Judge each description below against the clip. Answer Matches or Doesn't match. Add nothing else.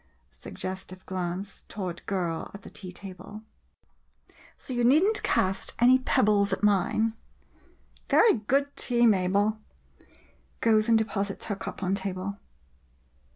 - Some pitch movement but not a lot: Matches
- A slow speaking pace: Matches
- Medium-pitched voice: Doesn't match